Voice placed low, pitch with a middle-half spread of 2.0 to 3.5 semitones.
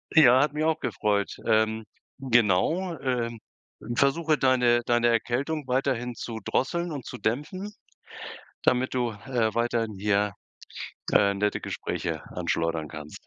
No: low, 120 Hz; average, 4.2 semitones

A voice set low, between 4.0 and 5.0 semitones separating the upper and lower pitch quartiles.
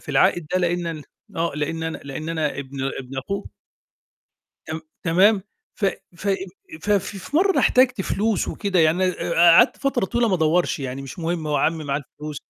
No: medium, 170 Hz; average, 4.4 semitones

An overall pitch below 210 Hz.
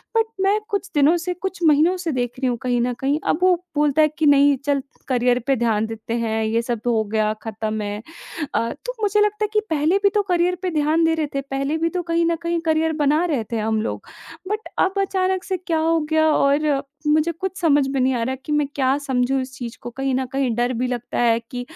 No: very high, 285 Hz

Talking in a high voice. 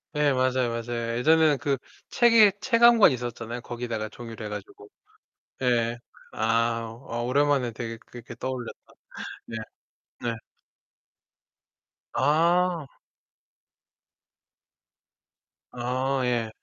No: low, 120 Hz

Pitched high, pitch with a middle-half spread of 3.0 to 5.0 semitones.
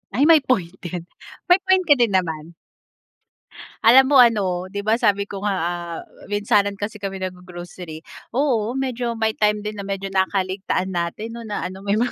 Yes: high, 205 Hz; average, 3.9 semitones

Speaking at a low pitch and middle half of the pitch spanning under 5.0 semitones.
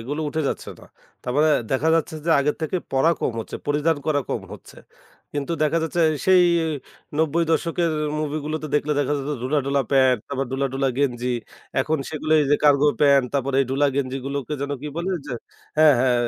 No: medium, 145 Hz; narrow, 2.4 semitones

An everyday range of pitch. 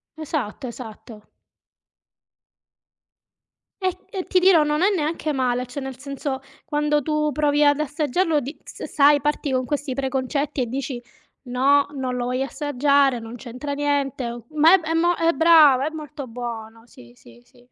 Yes: average, 3.2 semitones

